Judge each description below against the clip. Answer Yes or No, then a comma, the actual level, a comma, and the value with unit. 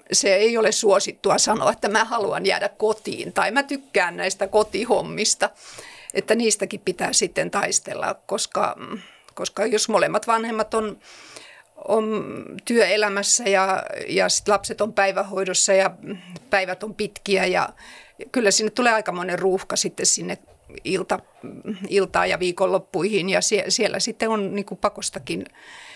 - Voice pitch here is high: Yes, high, 200 Hz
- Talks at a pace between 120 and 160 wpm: Yes, average, 135 wpm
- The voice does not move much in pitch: Yes, narrow, 2.0 semitones